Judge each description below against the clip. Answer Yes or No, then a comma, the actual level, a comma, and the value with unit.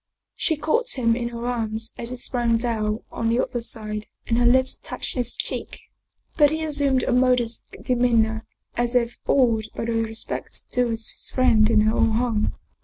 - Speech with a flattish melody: Yes, narrow, 2.0 semitones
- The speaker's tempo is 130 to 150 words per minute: No, average, 180 wpm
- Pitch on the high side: Yes, high, 235 Hz